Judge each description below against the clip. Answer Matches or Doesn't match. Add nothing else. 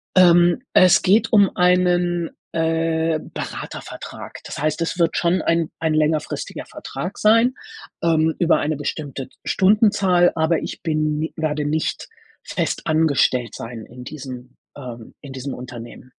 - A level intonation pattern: Doesn't match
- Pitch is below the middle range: Doesn't match